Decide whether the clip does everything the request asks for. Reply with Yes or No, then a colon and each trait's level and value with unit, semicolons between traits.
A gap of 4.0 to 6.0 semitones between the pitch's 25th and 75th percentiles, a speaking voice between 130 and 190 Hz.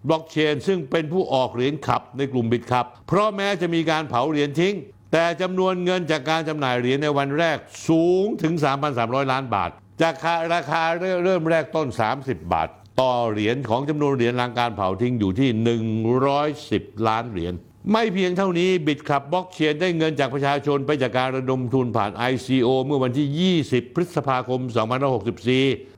Yes: average, 5.0 semitones; medium, 140 Hz